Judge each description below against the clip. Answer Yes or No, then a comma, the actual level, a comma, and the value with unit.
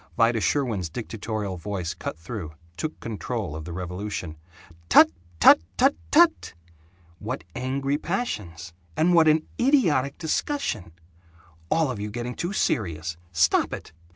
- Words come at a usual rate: No, slow, 130 wpm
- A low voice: Yes, low, 115 Hz